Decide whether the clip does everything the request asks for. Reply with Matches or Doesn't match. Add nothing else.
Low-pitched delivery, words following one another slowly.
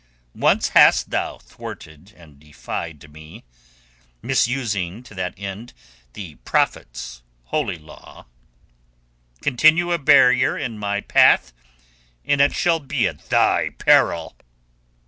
Matches